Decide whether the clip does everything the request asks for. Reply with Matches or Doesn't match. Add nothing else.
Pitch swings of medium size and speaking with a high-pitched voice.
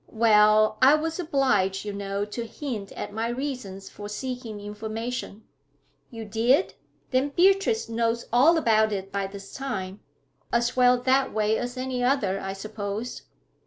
Matches